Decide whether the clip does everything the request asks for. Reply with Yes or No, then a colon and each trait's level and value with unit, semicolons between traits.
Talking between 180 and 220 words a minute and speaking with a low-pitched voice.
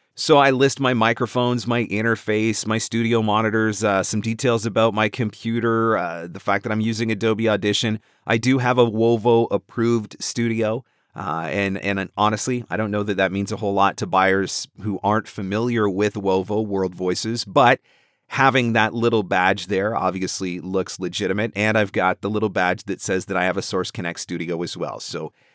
Yes: average, 190 wpm; low, 110 Hz